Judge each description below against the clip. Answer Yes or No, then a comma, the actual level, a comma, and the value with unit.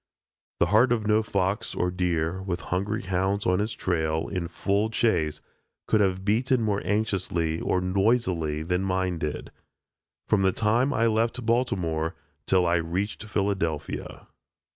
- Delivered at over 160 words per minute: No, average, 145 wpm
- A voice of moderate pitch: No, very low, 95 Hz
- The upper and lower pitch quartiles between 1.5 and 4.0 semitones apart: Yes, average, 3.6 semitones